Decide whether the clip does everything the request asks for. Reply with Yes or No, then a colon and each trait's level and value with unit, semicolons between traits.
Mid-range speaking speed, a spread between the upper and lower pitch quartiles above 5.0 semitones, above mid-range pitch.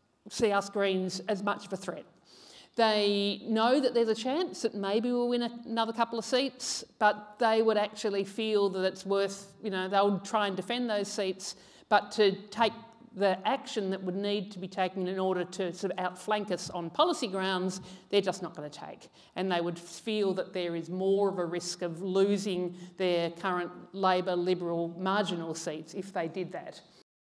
No: average, 195 wpm; average, 2.8 semitones; high, 195 Hz